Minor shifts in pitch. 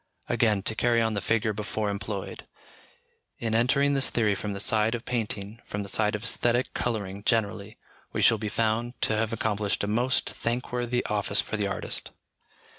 Yes: narrow, 2.3 semitones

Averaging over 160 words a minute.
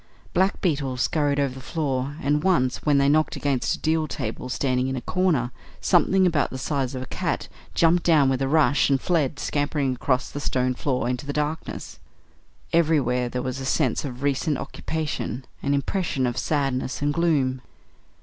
Yes: average, 180 wpm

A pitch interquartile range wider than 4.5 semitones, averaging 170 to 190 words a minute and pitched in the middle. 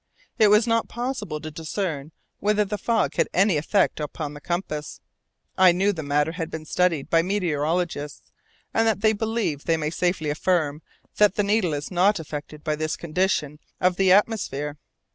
Yes: average, 5.1 semitones; average, 175 wpm; medium, 175 Hz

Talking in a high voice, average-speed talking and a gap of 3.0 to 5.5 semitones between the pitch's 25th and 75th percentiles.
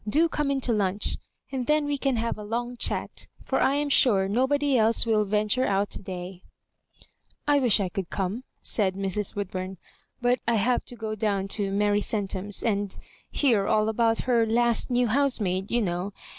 Yes: high, 220 Hz; average, 190 wpm; average, 3.9 semitones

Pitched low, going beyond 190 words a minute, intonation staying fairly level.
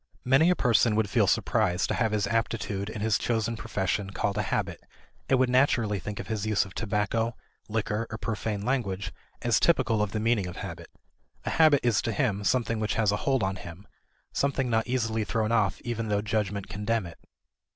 Yes: low, 110 Hz; average, 200 wpm; narrow, 2.3 semitones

